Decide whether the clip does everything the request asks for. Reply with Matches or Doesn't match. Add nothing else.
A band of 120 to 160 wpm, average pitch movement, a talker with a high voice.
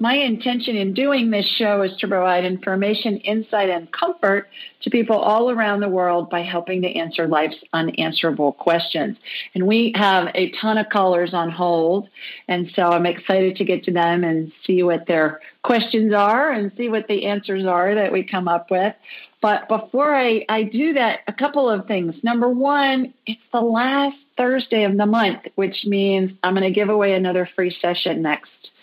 Doesn't match